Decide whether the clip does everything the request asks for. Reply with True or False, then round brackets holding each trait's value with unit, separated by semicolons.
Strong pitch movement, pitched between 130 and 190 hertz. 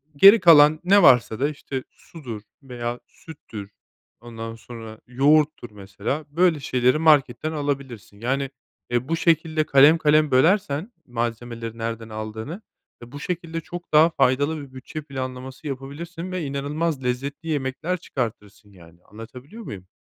False (4.8 semitones; 135 Hz)